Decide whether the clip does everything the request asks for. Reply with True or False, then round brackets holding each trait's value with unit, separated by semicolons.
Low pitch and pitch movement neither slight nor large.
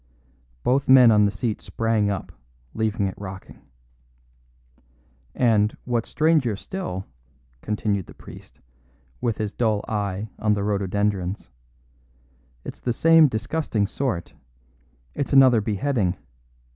True (110 Hz; 3.6 semitones)